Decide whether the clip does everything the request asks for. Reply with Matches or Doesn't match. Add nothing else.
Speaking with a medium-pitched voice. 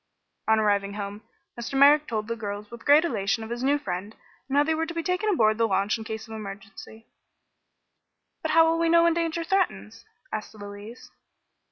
Doesn't match